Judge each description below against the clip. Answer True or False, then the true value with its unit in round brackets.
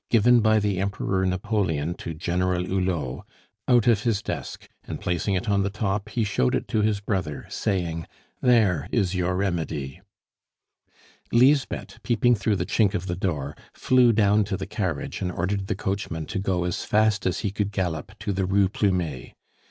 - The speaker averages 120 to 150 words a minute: False (175 wpm)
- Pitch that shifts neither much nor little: True (3.0 semitones)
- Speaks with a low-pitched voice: True (95 Hz)